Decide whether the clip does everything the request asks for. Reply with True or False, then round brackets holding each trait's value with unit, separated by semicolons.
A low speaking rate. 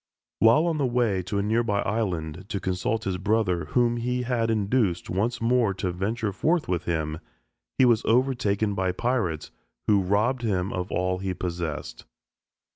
False (165 wpm)